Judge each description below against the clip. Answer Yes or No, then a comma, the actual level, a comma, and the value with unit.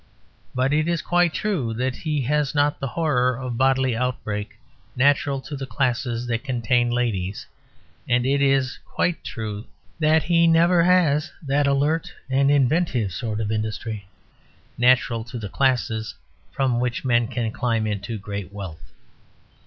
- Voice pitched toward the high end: No, low, 125 Hz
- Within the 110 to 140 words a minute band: No, average, 150 wpm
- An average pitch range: Yes, average, 4.1 semitones